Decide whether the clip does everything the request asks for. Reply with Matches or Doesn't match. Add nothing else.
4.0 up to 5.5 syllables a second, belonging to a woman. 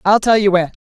Doesn't match